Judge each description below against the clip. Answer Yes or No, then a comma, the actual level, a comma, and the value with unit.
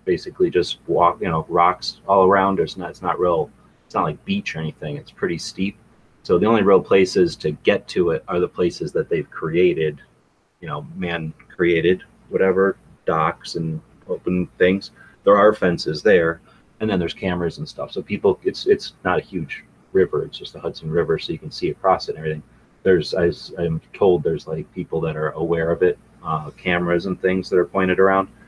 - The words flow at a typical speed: Yes, average, 190 wpm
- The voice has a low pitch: Yes, very low, 90 Hz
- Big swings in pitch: Yes, wide, 5.9 semitones